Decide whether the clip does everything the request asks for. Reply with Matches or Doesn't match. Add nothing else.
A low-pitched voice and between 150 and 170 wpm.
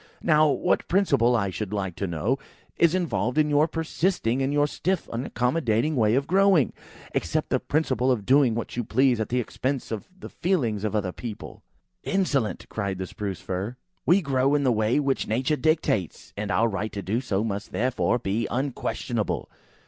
Doesn't match